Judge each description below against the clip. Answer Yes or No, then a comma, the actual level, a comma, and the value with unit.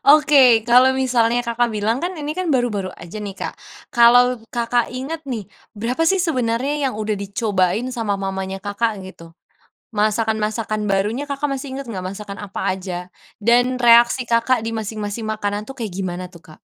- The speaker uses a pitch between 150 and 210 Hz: No, high, 230 Hz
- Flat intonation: No, average, 3.8 semitones